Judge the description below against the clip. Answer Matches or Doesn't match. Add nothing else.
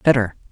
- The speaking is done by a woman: Matches